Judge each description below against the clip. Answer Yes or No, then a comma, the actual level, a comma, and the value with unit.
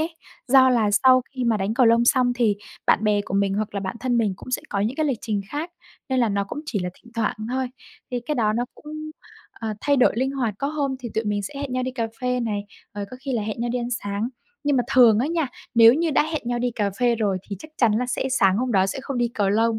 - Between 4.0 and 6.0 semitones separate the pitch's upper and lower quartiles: No, average, 3.6 semitones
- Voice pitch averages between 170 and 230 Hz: No, high, 240 Hz